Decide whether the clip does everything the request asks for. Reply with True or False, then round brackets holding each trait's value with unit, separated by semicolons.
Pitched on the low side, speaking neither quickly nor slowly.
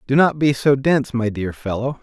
False (130 Hz; 240 wpm)